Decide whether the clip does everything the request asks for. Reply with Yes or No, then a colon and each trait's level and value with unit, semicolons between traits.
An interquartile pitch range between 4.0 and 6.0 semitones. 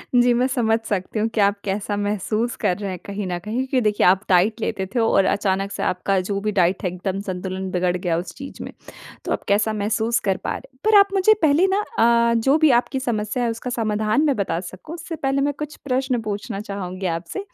Yes: average, 4.5 semitones